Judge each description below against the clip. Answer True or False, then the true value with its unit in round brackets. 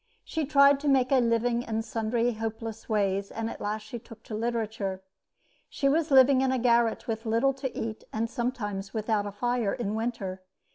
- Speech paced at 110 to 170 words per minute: False (190 wpm)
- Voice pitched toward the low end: False (230 Hz)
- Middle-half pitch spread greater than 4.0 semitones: False (2.5 semitones)